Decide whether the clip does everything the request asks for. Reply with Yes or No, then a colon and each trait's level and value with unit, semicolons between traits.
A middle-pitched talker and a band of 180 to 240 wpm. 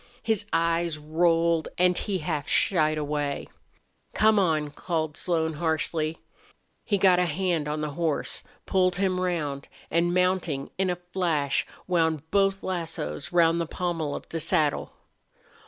No: medium, 165 Hz; average, 140 wpm